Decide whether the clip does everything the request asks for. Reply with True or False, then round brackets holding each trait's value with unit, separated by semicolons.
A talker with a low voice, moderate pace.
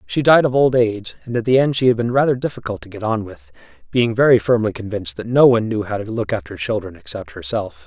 False (110 Hz; 250 wpm)